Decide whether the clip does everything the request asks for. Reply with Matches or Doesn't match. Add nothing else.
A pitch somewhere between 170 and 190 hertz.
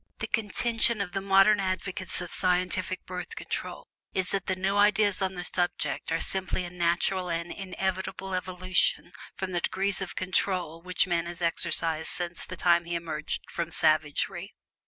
Matches